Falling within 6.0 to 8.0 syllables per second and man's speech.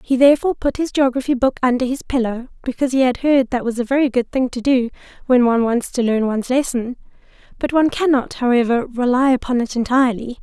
No: 6.2 syllables/s; female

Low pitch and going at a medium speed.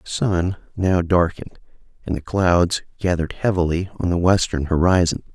Yes: very low, 90 Hz; average, 145 wpm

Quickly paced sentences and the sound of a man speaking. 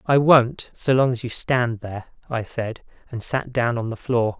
Yes: fast, 220 wpm; male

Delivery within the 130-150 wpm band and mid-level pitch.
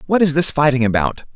No: fast, 220 wpm; medium, 145 Hz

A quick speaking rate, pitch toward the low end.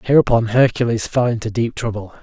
No: average, 160 wpm; low, 115 Hz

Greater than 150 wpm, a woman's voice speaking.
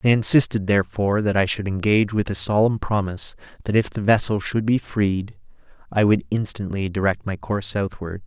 No: average, 180 wpm; male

